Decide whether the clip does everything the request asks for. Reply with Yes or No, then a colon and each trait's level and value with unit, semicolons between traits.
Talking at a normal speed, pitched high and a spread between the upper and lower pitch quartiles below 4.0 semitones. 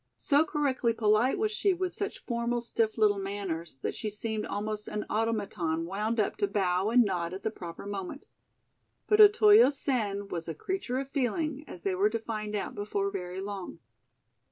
No: average, 180 wpm; high, 215 Hz; average, 4.5 semitones